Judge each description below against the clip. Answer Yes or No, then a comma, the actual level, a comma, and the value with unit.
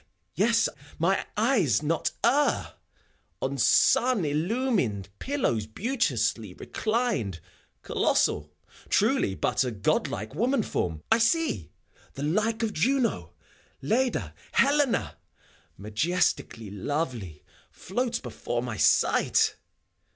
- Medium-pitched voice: Yes, medium, 175 Hz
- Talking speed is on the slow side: Yes, slow, 105 wpm